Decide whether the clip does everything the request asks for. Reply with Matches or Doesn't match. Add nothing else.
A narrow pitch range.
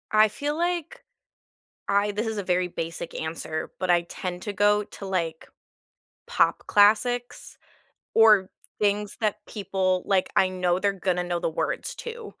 Doesn't match